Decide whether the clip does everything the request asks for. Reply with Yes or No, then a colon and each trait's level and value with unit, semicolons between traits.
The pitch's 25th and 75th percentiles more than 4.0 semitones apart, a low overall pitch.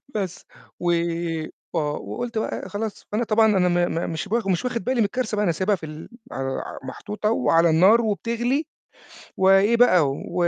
No: average, 4.6 semitones; high, 205 Hz